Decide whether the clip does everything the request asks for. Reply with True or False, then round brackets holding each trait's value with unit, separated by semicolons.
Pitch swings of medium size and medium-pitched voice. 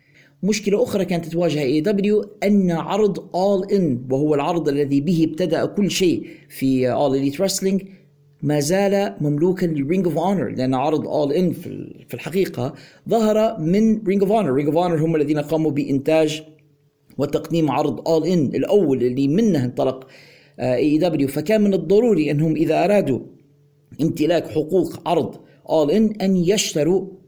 True (4.8 semitones; 160 Hz)